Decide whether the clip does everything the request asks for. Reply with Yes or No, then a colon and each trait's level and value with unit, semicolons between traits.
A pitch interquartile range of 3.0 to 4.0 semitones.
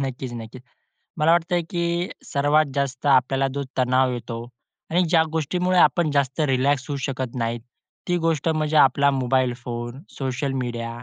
Yes: average, 3.5 semitones